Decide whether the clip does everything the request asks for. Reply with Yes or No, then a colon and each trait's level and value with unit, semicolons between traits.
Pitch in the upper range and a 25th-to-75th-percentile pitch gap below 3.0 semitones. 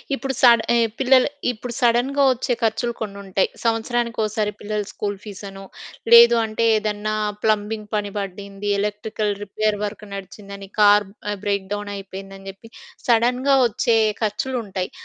Yes: high, 210 Hz; narrow, 2.6 semitones